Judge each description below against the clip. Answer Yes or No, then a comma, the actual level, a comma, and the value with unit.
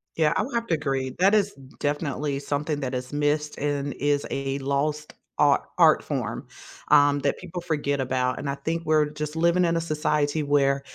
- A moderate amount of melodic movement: No, narrow, 2.2 semitones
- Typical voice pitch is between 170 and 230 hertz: No, medium, 145 Hz